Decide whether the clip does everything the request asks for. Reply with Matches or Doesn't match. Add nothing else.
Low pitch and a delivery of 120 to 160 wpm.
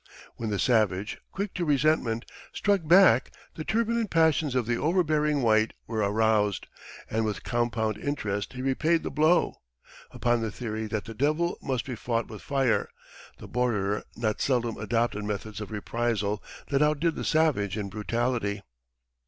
Matches